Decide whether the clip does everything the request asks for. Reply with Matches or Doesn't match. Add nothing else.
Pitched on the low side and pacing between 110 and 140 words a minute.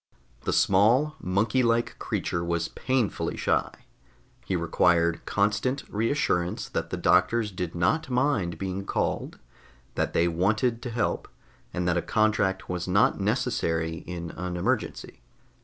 Matches